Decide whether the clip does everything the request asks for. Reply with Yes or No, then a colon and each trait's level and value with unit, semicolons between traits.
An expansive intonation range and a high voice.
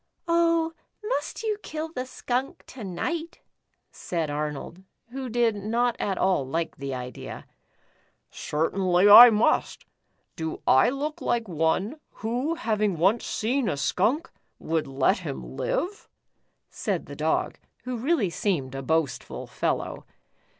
Yes: wide, 8.8 semitones; high, 215 Hz